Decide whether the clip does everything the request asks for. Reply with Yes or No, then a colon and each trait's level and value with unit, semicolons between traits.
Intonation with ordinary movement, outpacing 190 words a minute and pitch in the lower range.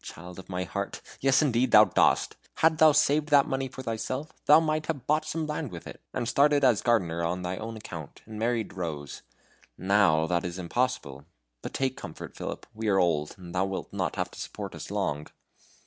No: wide, 7.5 semitones; fast, 205 wpm; low, 110 Hz